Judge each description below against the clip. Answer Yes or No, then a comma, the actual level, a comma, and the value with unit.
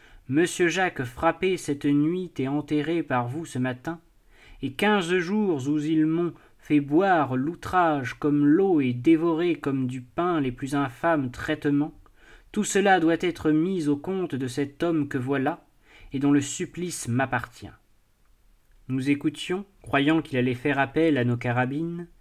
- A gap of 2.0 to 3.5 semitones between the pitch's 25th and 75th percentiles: No, average, 3.9 semitones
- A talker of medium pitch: Yes, medium, 150 Hz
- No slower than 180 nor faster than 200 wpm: No, average, 155 wpm